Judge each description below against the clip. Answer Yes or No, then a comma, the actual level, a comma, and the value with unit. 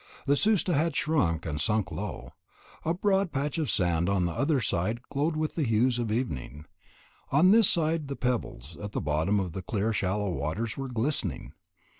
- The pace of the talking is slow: No, average, 185 wpm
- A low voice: Yes, low, 115 Hz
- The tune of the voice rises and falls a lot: Yes, wide, 8.5 semitones